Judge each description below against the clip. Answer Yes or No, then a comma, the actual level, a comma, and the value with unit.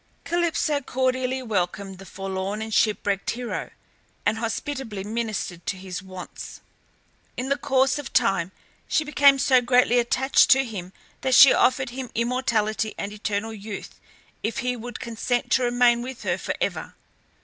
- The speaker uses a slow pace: No, average, 150 wpm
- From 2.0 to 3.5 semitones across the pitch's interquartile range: No, average, 4.0 semitones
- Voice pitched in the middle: No, high, 240 Hz